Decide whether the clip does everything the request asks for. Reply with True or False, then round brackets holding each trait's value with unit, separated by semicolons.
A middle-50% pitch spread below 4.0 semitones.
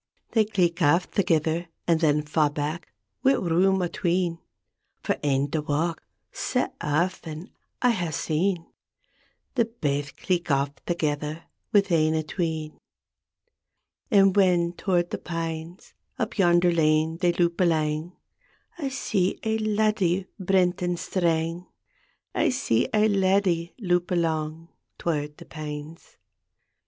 True (3.1 semitones)